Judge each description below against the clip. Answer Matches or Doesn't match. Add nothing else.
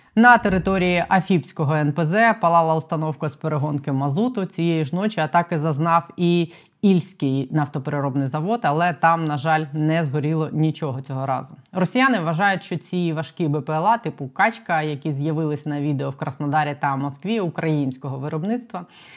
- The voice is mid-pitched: Matches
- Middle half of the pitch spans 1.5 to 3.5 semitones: Matches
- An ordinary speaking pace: Matches